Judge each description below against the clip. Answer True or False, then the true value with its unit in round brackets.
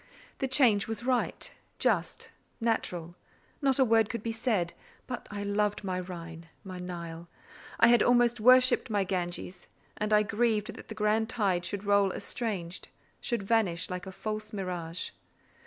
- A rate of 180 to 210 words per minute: False (155 wpm)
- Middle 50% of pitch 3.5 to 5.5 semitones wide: True (4.0 semitones)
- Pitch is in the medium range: False (210 Hz)